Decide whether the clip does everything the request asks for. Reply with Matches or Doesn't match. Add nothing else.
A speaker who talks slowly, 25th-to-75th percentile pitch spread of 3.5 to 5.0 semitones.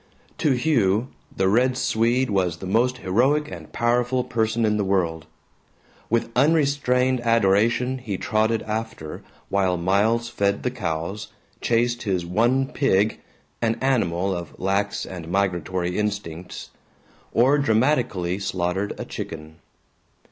Matches